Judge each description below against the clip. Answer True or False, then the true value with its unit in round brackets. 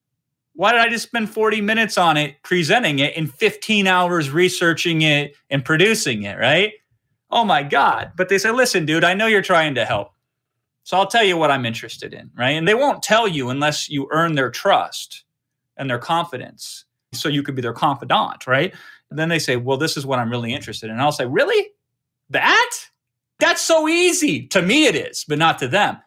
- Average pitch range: False (8.0 semitones)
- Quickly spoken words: True (210 wpm)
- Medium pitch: True (160 Hz)